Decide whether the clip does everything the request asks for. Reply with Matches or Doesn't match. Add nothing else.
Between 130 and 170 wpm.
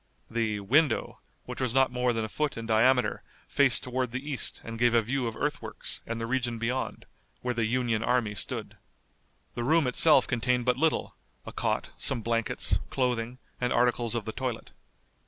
Doesn't match